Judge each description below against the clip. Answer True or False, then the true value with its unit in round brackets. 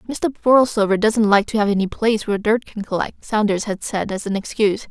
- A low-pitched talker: False (210 Hz)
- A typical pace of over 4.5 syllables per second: True (5.8 syllables/s)